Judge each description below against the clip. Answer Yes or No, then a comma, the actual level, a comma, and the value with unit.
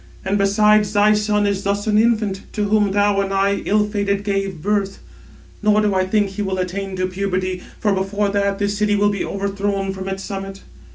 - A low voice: No, high, 200 Hz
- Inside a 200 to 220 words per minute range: Yes, fast, 205 wpm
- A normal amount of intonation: No, narrow, 1.2 semitones